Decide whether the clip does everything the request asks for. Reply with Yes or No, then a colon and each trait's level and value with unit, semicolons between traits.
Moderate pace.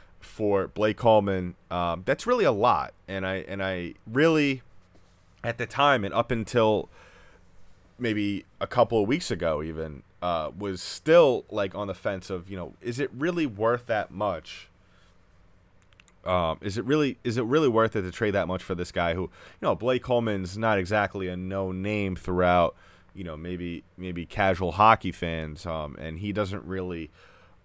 Yes: average, 175 wpm